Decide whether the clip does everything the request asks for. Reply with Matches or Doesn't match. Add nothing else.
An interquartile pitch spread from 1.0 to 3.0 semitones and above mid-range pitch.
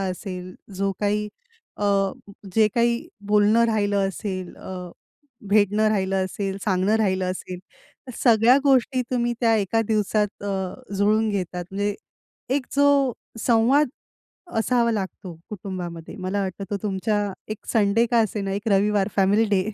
Matches